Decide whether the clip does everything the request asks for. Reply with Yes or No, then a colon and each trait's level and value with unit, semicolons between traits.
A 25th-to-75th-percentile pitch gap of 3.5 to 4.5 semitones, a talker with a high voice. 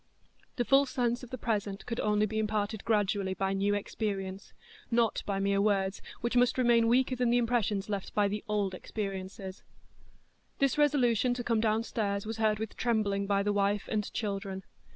No: average, 3.0 semitones; high, 215 Hz